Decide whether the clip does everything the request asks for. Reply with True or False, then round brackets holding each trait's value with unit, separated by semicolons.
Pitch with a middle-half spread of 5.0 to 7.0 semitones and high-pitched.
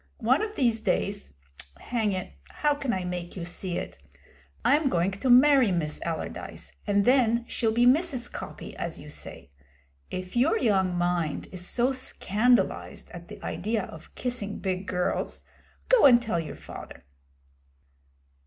True (5.6 semitones; 220 Hz)